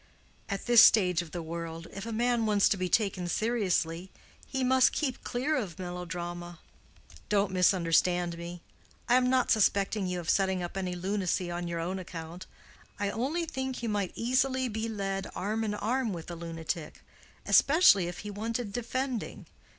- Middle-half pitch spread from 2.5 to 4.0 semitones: No, average, 4.8 semitones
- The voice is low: No, high, 195 Hz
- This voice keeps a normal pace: Yes, average, 170 wpm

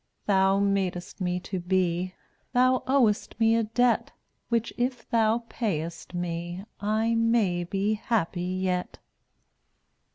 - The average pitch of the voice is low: No, high, 200 Hz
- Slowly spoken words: Yes, slow, 125 wpm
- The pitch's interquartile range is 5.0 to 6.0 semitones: No, average, 4.2 semitones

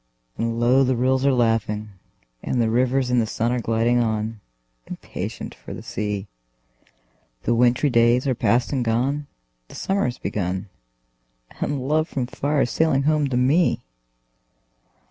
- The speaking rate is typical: Yes, average, 155 wpm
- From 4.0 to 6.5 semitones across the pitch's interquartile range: No, average, 2.9 semitones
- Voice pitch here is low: Yes, low, 125 Hz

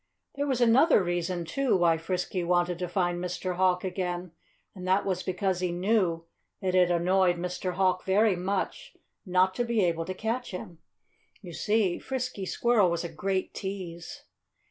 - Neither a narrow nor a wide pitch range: No, narrow, 2.0 semitones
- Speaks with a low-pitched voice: No, medium, 185 Hz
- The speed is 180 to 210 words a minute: No, average, 165 wpm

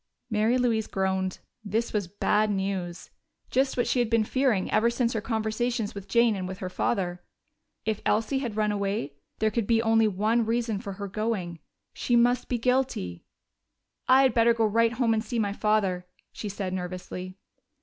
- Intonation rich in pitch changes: No, average, 3.3 semitones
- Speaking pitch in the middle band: No, high, 215 Hz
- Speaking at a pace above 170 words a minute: Yes, average, 180 wpm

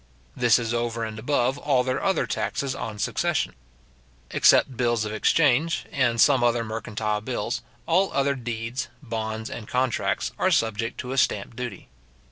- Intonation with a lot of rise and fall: No, average, 2.7 semitones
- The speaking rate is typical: Yes, average, 155 wpm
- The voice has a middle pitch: No, low, 120 Hz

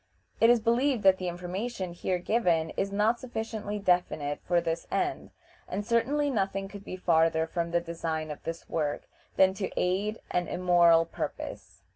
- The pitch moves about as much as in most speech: Yes, average, 4.2 semitones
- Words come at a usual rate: Yes, average, 165 wpm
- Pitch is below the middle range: No, medium, 185 Hz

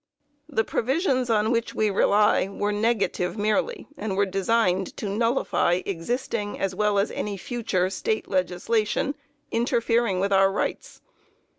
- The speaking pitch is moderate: No, high, 210 Hz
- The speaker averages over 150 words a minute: No, slow, 135 wpm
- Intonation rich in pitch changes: No, average, 3.1 semitones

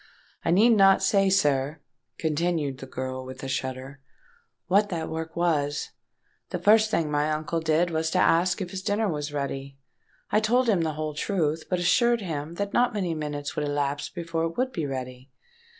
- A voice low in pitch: No, medium, 160 Hz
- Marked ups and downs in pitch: No, average, 4.8 semitones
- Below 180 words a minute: No, average, 185 wpm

